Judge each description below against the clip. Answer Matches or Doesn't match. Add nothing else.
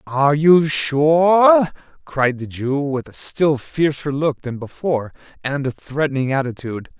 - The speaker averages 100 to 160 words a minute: Matches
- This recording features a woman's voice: Doesn't match